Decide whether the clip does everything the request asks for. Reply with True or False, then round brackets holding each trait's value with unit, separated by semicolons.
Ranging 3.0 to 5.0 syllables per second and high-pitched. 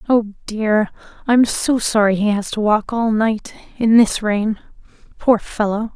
True (3.9 syllables/s; 215 Hz)